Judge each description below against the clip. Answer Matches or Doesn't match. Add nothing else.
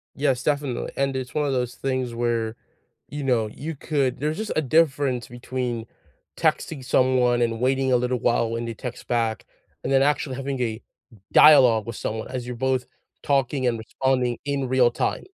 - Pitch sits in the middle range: Doesn't match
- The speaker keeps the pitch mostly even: Matches